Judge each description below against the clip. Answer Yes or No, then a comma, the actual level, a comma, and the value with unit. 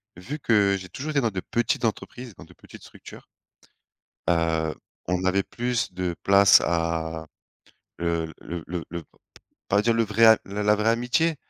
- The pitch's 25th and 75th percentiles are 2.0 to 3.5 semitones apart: No, average, 5.1 semitones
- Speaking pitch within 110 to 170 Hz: No, low, 100 Hz